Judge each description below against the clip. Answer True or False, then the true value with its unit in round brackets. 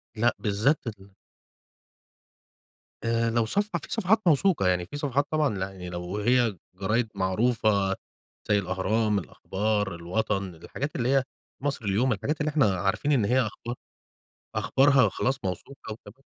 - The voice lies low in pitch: True (110 Hz)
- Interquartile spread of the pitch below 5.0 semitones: False (5.5 semitones)